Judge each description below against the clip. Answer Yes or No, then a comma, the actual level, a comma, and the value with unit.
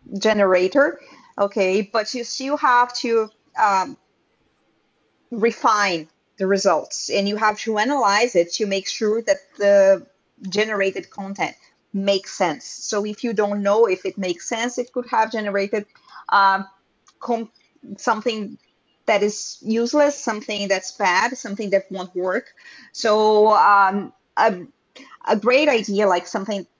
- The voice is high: Yes, high, 210 Hz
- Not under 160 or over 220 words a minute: No, slow, 135 wpm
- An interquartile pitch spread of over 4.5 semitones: No, average, 3.0 semitones